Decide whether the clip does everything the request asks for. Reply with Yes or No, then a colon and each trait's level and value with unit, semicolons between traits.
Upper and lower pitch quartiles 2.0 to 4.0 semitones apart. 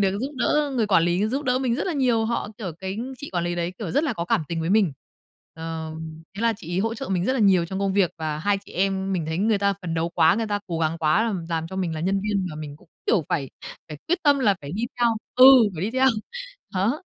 No: average, 5.3 semitones